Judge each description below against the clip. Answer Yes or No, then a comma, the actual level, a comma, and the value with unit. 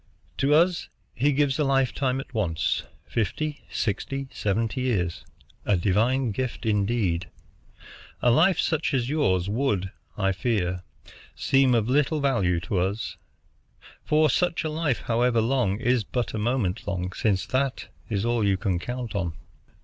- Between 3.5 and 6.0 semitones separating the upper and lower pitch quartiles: Yes, wide, 5.4 semitones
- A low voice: Yes, low, 120 Hz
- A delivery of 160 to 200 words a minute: No, average, 150 wpm